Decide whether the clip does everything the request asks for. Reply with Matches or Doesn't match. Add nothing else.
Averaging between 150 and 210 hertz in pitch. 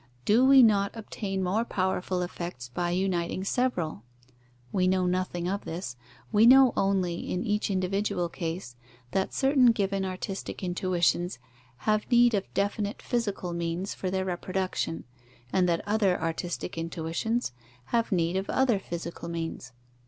Matches